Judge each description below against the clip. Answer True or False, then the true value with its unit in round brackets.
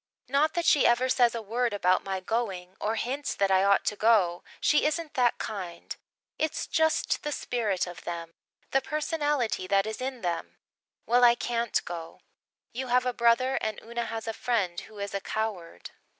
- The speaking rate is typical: True (185 wpm)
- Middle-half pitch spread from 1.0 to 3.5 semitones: False (4.4 semitones)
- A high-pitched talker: True (230 Hz)